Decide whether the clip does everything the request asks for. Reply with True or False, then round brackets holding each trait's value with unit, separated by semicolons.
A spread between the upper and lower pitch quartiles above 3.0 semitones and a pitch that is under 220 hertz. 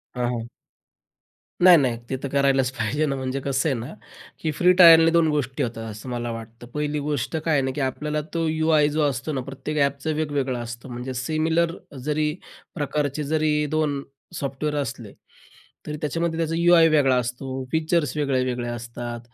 True (3.5 semitones; 140 Hz)